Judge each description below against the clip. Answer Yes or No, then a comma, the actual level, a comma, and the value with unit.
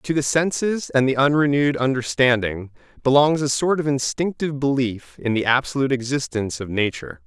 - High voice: No, low, 135 Hz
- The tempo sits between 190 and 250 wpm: No, average, 155 wpm